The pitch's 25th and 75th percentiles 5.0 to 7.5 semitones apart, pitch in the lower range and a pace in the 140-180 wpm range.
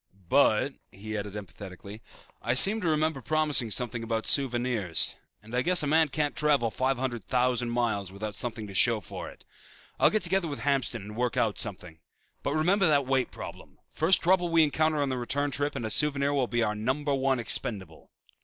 No: average, 5.3 semitones; low, 125 Hz; average, 195 wpm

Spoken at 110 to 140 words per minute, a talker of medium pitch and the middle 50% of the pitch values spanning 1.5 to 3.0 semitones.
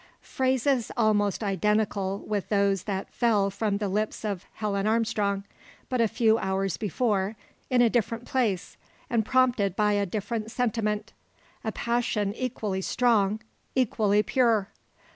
No: slow, 135 wpm; high, 215 Hz; average, 2.7 semitones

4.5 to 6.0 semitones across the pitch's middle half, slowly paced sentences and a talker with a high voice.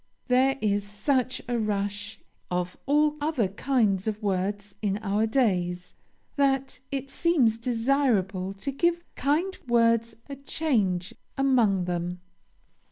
Yes: wide, 5.5 semitones; slow, 120 wpm; high, 225 Hz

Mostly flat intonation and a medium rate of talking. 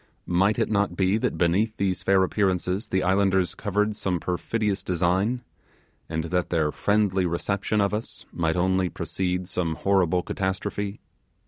Yes: narrow, 2.3 semitones; average, 145 wpm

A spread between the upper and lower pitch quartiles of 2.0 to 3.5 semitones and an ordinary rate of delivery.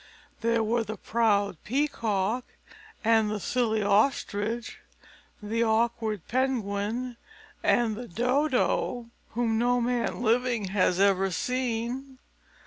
No: average, 2.7 semitones; slow, 105 wpm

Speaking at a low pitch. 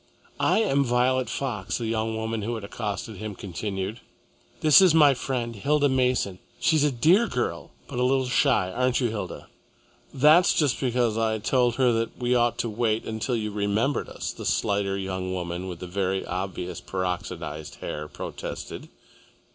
Yes: low, 115 Hz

